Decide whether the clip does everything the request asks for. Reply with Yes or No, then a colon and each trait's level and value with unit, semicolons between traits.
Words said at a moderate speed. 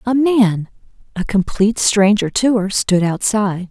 No: slow, 115 wpm